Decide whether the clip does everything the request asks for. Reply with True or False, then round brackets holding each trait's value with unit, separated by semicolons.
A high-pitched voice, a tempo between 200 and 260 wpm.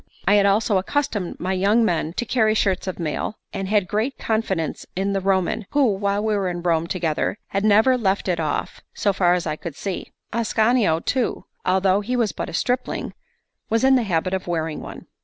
True (195 Hz; 205 wpm)